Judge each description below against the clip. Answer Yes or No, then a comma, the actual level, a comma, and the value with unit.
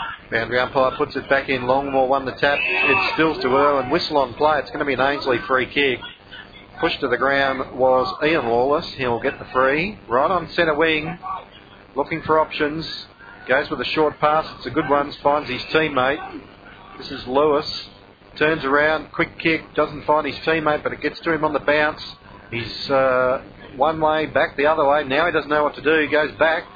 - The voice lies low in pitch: No, medium, 145 Hz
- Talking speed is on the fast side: Yes, fast, 210 wpm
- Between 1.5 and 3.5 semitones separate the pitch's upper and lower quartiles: Yes, average, 2.9 semitones